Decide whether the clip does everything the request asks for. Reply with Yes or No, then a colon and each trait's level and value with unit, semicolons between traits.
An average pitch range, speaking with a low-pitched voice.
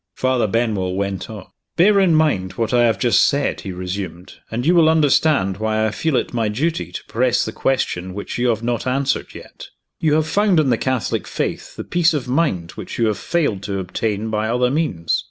No: wide, 6.7 semitones; low, 120 Hz